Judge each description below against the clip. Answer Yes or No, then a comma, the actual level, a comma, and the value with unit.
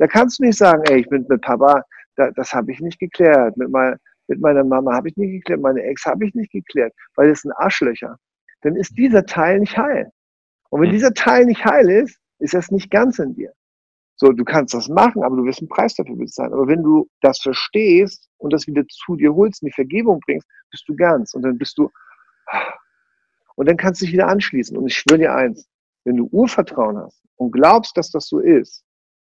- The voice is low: No, medium, 170 Hz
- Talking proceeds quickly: Yes, fast, 220 wpm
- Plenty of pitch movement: Yes, wide, 8.2 semitones